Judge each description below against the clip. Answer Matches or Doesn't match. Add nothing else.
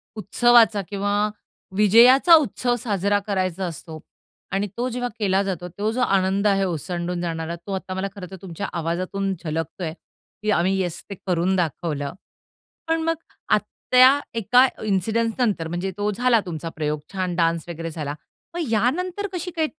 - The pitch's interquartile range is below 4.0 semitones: Doesn't match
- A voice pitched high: Matches